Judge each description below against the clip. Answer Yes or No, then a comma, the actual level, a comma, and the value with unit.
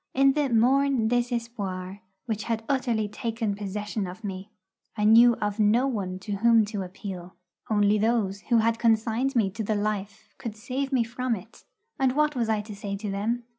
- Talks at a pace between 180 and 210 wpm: Yes, average, 185 wpm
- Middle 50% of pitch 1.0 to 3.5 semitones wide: Yes, average, 2.8 semitones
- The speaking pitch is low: No, high, 220 Hz